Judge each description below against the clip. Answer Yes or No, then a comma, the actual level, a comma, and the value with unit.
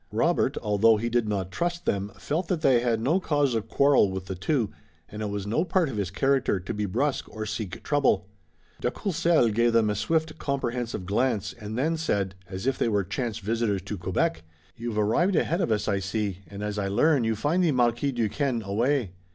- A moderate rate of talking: No, fast, 210 wpm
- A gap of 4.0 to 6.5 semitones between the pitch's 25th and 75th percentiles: Yes, average, 5.3 semitones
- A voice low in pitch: Yes, low, 115 Hz